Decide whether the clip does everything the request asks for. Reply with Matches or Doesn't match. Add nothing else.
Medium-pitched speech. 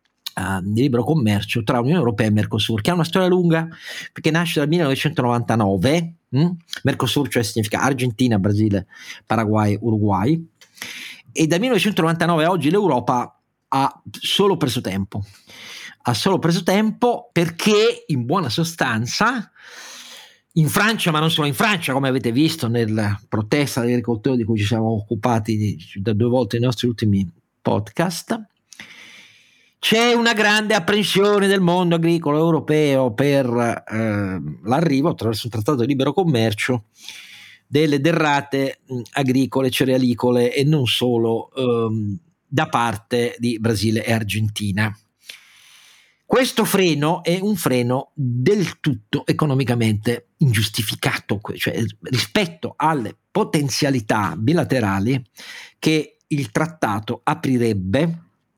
Doesn't match